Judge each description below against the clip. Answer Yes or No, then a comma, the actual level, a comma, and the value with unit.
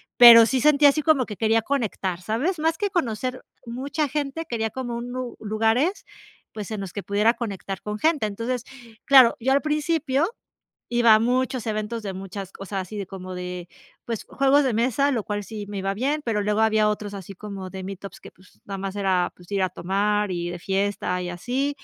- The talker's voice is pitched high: Yes, high, 220 Hz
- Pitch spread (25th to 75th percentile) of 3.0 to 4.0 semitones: No, average, 4.7 semitones